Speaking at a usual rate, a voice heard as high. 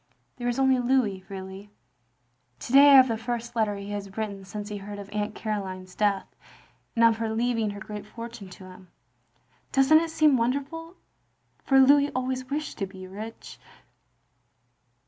Yes: average, 165 wpm; high, 225 Hz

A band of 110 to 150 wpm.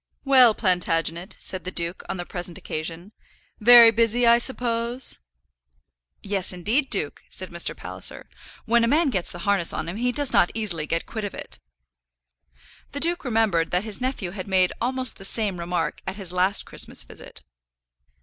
No: average, 170 wpm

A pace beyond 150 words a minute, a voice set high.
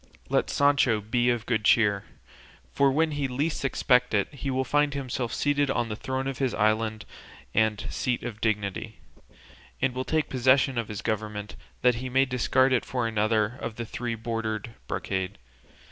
No: average, 170 wpm; low, 120 Hz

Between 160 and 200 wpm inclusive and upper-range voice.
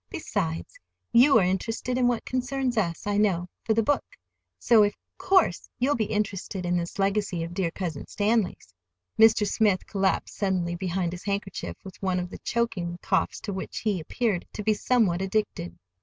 Yes: average, 170 wpm; high, 200 Hz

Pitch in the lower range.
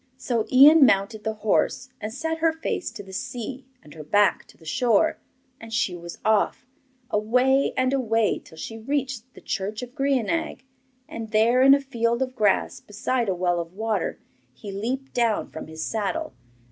No: high, 230 Hz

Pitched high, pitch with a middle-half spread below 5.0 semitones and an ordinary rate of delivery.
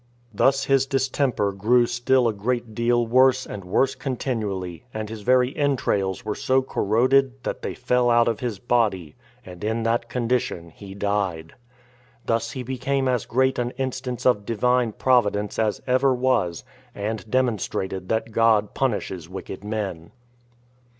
No: low, 115 Hz; average, 3.8 semitones; average, 150 wpm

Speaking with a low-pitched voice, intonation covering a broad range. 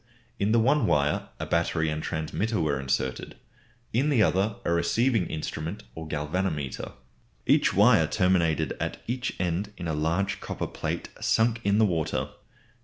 Yes: very low, 90 Hz; wide, 5.7 semitones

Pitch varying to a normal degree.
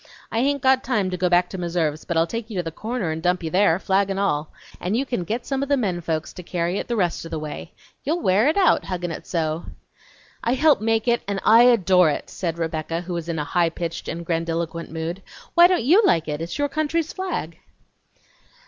No: wide, 6.3 semitones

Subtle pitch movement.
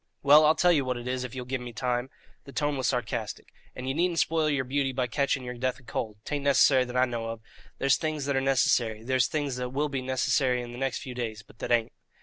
Yes: narrow, 2.3 semitones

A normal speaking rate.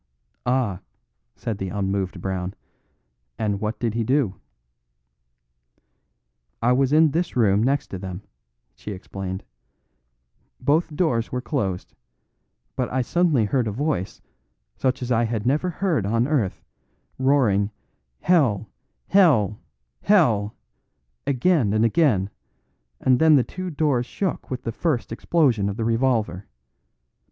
No: slow, 125 wpm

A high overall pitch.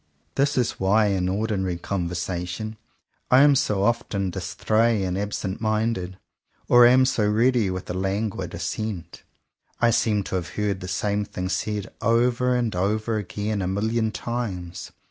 No: low, 105 Hz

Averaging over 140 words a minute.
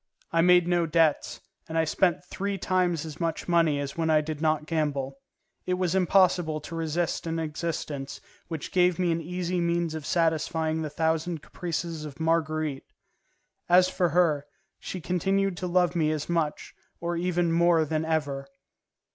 Yes: average, 165 wpm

